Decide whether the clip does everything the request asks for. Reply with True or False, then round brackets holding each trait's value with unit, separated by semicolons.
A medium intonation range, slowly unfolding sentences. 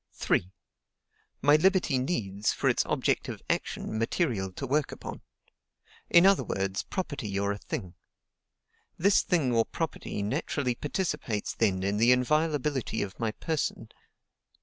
False (7.1 semitones; 130 wpm)